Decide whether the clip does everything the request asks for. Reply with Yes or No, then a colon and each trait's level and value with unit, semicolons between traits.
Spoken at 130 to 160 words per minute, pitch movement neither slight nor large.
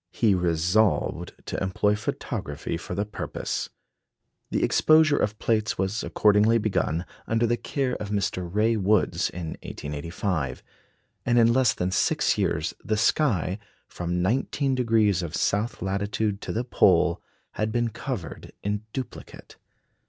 Yes: slow, 135 wpm; average, 4.2 semitones